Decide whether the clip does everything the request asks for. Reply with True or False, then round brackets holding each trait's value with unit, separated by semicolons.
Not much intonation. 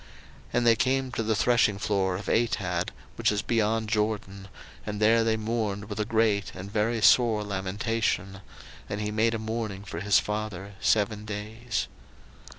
True (2.0 semitones)